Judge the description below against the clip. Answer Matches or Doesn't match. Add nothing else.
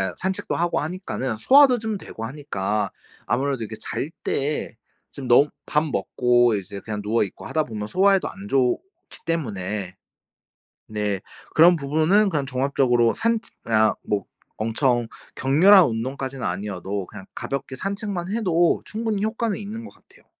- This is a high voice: Doesn't match